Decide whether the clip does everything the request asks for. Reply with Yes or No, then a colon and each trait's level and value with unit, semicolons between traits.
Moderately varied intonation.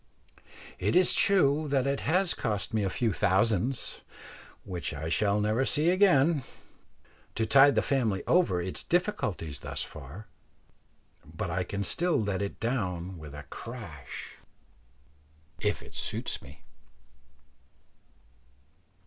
No: wide, 7.5 semitones